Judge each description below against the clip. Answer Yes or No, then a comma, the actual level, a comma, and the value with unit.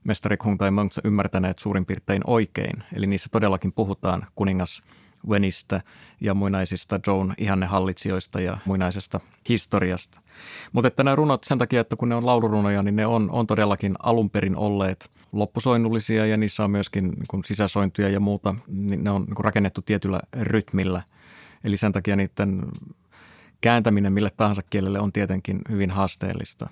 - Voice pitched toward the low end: Yes, low, 100 Hz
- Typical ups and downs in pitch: No, narrow, 2.0 semitones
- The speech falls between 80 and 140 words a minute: No, average, 150 wpm